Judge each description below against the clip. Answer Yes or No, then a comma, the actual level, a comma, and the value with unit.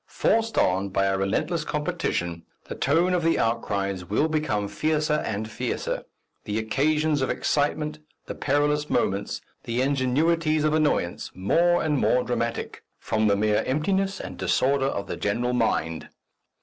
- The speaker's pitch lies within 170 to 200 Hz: No, low, 130 Hz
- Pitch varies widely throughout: Yes, wide, 7.0 semitones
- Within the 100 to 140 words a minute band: No, average, 150 wpm